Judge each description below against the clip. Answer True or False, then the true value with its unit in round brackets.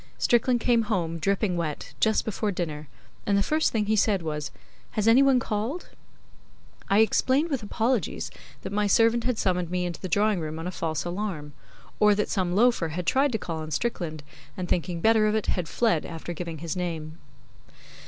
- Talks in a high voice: True (195 Hz)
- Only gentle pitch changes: False (4.9 semitones)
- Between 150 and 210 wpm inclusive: True (195 wpm)